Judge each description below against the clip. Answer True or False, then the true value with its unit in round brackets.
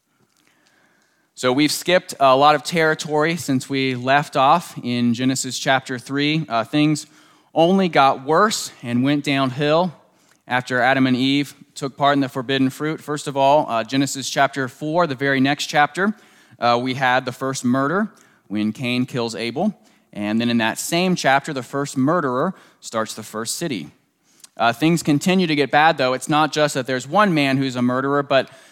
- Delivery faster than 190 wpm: False (180 wpm)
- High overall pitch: False (140 Hz)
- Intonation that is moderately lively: True (3.0 semitones)